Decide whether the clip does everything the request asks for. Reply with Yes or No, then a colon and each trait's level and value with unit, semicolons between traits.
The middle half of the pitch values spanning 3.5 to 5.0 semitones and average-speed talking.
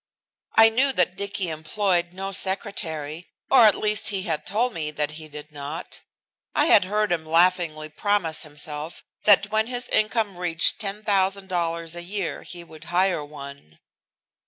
Yes: average, 4.4 semitones; average, 155 wpm